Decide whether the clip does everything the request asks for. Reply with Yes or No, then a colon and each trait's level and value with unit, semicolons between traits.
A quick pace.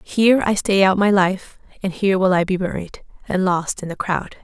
Yes: fast, 230 wpm